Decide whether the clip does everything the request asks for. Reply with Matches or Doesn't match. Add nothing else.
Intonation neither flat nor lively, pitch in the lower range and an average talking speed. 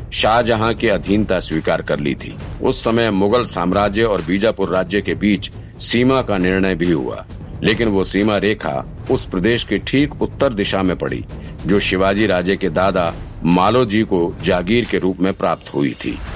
Matches